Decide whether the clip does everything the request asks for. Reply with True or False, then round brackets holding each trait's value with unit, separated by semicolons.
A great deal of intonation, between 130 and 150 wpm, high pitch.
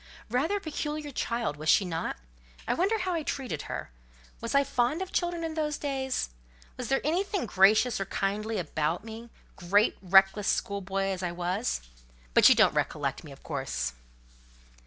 False (7.9 semitones; 165 wpm; 225 Hz)